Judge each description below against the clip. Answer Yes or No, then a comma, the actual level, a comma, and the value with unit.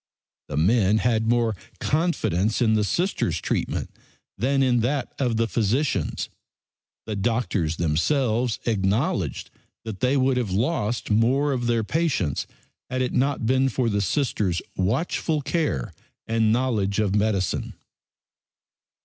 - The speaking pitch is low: Yes, low, 115 Hz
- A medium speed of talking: No, slow, 130 wpm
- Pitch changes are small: No, average, 4.3 semitones